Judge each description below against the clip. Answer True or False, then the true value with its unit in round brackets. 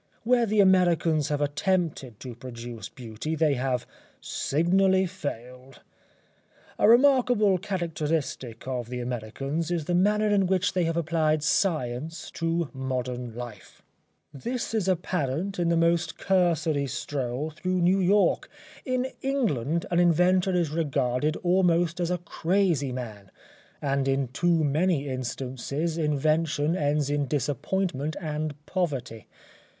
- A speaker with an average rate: False (125 wpm)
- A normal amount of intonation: True (5.0 semitones)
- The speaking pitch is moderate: True (155 Hz)